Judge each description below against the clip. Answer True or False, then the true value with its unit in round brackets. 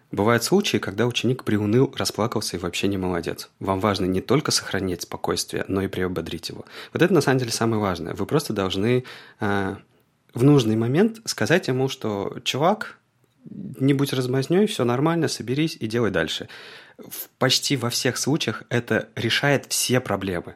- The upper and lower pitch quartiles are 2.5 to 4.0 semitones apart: False (5.0 semitones)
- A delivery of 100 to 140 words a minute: False (160 wpm)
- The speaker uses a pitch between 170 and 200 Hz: False (120 Hz)